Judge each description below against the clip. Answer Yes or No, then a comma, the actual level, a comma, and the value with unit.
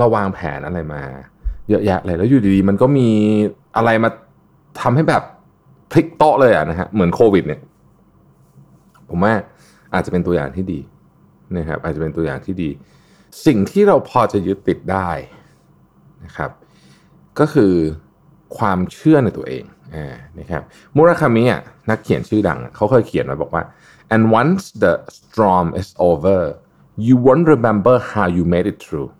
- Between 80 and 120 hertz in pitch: Yes, low, 100 Hz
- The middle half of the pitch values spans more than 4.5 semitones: Yes, average, 5.2 semitones